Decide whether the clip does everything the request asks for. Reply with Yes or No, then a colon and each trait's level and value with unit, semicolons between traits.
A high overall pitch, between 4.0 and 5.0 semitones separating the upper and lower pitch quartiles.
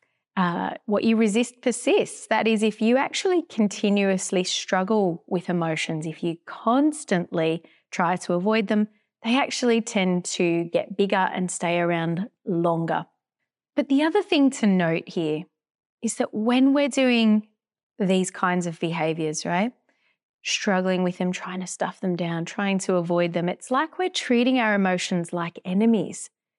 Yes: high, 195 Hz; average, 4.6 semitones